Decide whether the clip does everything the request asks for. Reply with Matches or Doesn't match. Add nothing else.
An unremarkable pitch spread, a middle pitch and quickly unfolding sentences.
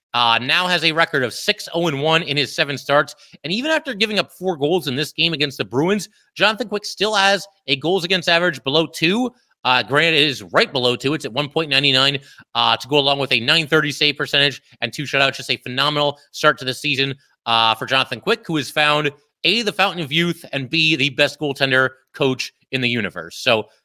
Matches